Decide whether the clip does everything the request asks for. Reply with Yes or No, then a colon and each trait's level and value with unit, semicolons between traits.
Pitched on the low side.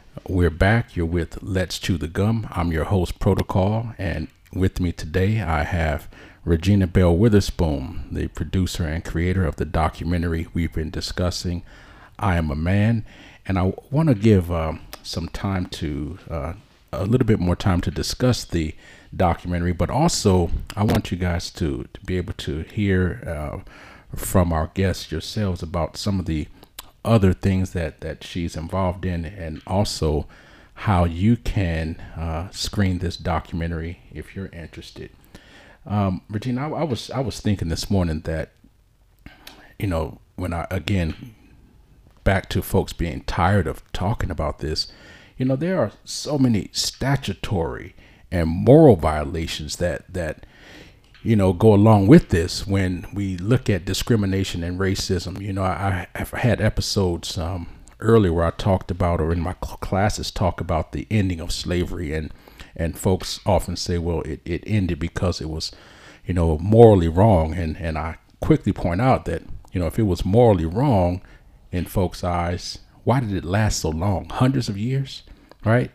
Yes: very low, 95 Hz